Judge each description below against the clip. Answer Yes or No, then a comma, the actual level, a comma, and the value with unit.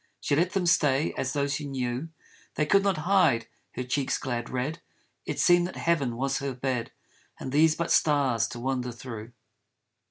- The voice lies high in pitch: No, low, 135 Hz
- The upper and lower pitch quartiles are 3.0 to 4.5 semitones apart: Yes, average, 4.2 semitones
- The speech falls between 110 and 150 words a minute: No, average, 180 wpm